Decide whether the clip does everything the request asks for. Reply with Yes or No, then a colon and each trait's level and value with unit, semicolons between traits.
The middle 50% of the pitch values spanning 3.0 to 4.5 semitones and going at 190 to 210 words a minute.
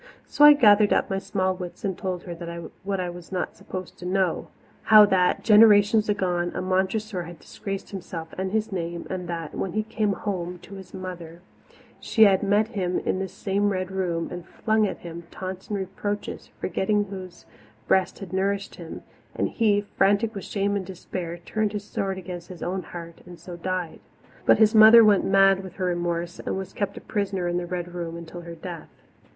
No: narrow, 2.5 semitones; average, 200 wpm